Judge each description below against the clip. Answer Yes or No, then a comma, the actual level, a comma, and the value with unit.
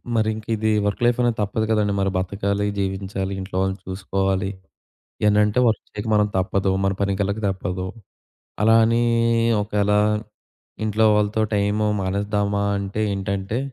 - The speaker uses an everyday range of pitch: No, narrow, 1.6 semitones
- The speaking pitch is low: Yes, low, 100 Hz